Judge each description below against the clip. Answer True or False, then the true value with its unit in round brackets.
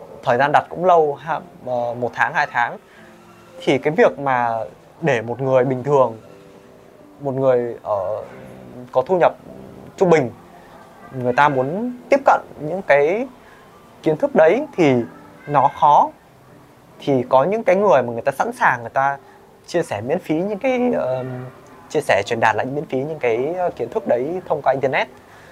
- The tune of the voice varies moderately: False (6.5 semitones)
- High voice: False (135 Hz)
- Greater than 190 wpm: False (175 wpm)